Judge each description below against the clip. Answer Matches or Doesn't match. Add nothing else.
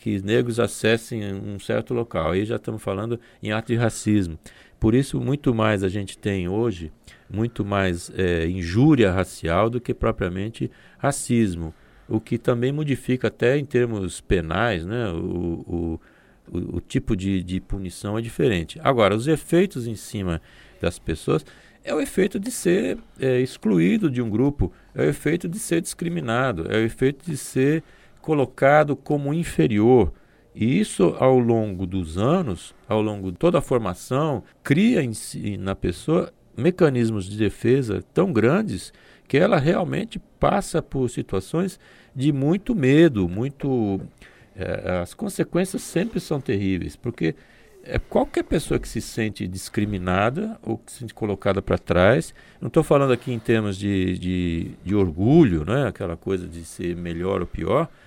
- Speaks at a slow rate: Doesn't match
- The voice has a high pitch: Doesn't match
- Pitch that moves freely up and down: Matches